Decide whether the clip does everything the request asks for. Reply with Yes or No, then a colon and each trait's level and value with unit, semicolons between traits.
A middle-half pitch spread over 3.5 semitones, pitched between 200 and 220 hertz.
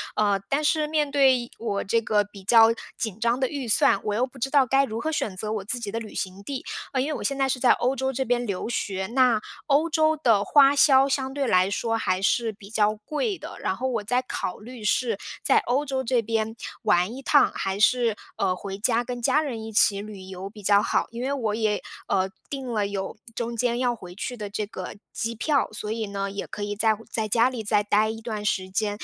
No: average, 4.1 semitones; high, 230 Hz